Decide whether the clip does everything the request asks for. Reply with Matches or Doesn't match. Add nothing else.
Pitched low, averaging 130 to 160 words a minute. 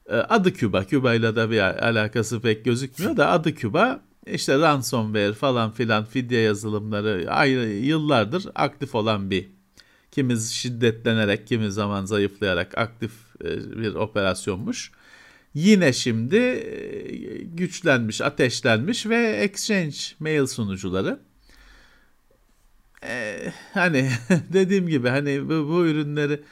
Doesn't match